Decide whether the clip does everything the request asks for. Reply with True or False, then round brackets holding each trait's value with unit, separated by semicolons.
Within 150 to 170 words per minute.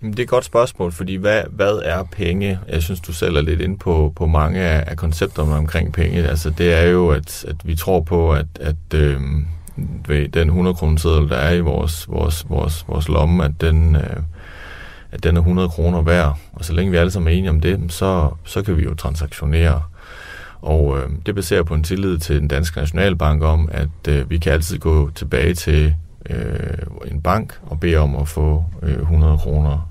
False (205 wpm)